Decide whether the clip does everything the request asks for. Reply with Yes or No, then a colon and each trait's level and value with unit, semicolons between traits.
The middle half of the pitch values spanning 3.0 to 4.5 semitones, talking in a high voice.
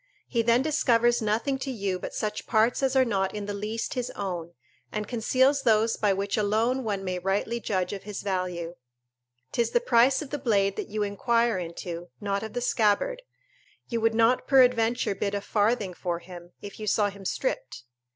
Yes: average, 3.4 semitones; high, 215 Hz